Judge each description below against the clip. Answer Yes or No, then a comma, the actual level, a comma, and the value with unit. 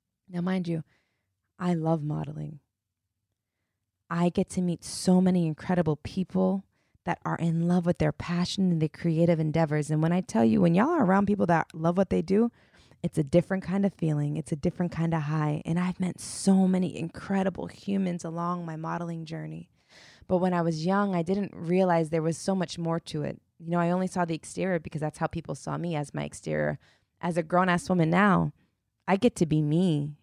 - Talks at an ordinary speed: No, fast, 210 wpm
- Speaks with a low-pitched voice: No, medium, 170 Hz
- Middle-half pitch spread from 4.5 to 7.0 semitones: No, average, 2.7 semitones